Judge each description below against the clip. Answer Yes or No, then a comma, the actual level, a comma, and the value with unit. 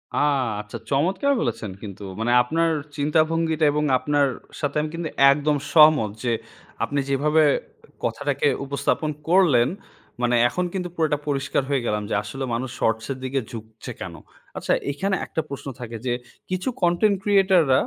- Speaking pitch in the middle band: Yes, medium, 145 Hz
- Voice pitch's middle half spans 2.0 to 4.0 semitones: No, average, 5.3 semitones